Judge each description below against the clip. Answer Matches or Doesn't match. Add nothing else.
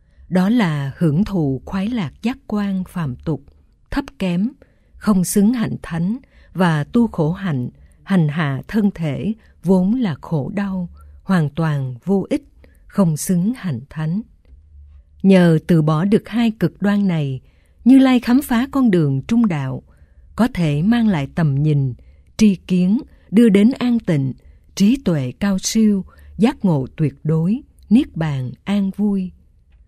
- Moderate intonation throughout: Doesn't match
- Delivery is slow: Matches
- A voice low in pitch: Doesn't match